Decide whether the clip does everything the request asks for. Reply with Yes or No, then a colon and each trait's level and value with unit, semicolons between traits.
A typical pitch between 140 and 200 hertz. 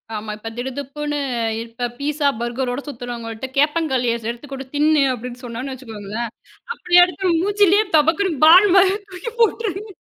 No: very high, 280 Hz